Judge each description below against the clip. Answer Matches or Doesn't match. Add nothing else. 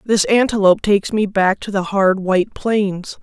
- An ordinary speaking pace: Matches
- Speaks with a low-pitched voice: Doesn't match